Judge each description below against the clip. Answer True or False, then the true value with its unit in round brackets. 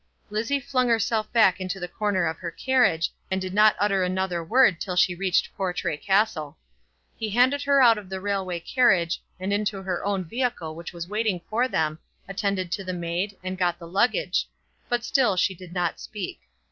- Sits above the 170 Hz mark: True (190 Hz)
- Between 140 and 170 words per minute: False (190 wpm)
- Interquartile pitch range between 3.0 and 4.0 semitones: True (3.4 semitones)